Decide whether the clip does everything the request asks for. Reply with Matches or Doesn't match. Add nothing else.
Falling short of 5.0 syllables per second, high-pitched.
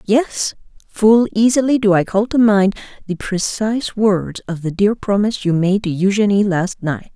Matches